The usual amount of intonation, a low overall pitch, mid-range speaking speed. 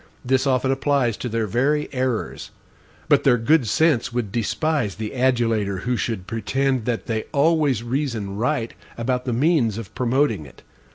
Yes: average, 3.2 semitones; low, 125 Hz; average, 160 wpm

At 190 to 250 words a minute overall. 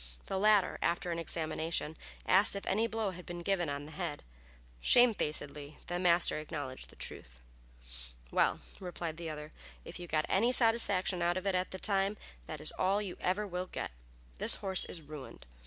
No: average, 180 wpm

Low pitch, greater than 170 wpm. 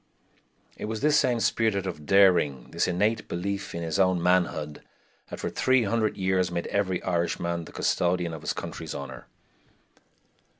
No: very low, 95 Hz; average, 160 wpm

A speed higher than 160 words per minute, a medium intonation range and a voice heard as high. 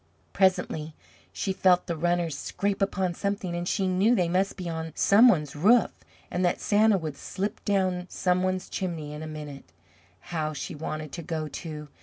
No: average, 180 wpm; average, 3.5 semitones; medium, 175 Hz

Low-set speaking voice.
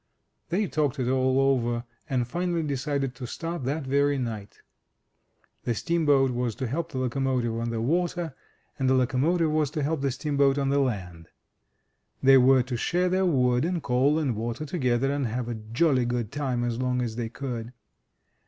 Yes: low, 130 Hz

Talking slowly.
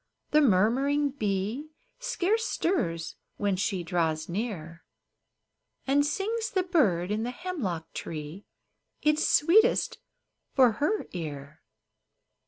Yes: slow, 105 wpm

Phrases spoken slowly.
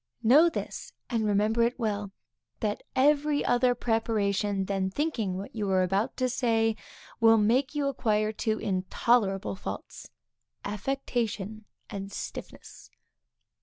Yes: slow, 125 wpm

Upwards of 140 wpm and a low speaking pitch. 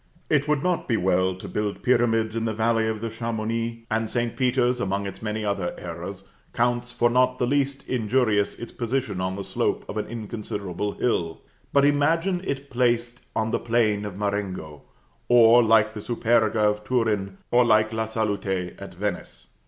Yes: average, 175 wpm; low, 115 Hz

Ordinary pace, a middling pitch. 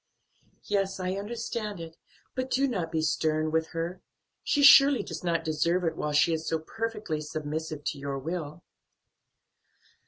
Yes: average, 155 wpm; medium, 165 Hz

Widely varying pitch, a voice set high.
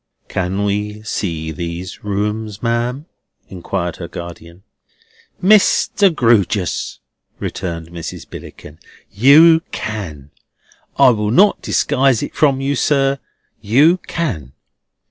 No: wide, 7.6 semitones; low, 105 Hz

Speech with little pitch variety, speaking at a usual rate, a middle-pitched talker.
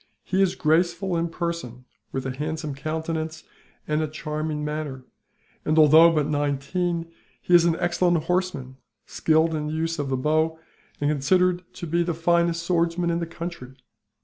Yes: narrow, 2.1 semitones; average, 165 wpm; medium, 160 Hz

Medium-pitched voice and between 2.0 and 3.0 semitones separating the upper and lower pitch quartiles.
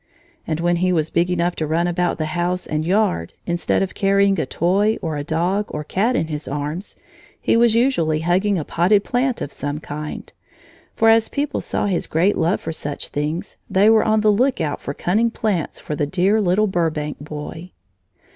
No: medium, 175 Hz; average, 4.7 semitones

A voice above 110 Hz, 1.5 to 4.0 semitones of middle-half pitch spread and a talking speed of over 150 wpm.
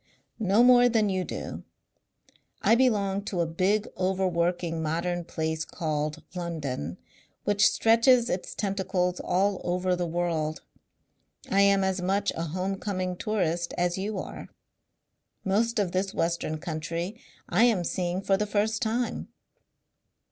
No: medium, 185 Hz; average, 3.1 semitones; slow, 135 wpm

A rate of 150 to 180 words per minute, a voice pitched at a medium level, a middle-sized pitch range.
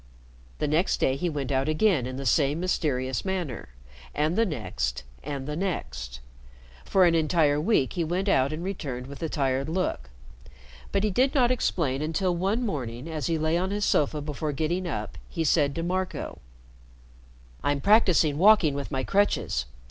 Yes: average, 175 wpm; medium, 155 Hz; average, 5.0 semitones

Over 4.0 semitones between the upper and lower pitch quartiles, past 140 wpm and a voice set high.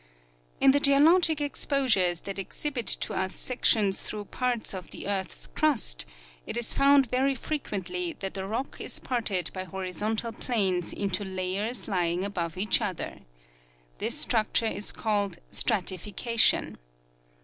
No: average, 5.1 semitones; slow, 135 wpm; high, 210 Hz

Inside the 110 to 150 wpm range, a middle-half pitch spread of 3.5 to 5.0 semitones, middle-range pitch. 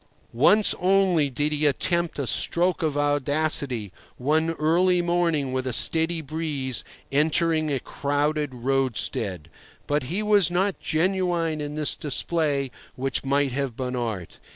Yes: slow, 135 wpm; average, 3.9 semitones; medium, 150 Hz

